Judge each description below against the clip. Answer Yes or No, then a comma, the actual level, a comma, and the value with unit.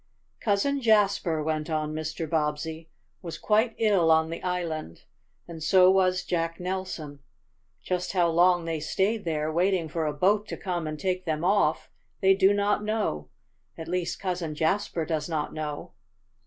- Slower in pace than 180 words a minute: Yes, average, 160 wpm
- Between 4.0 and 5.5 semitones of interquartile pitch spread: No, average, 3.3 semitones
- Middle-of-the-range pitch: Yes, medium, 170 Hz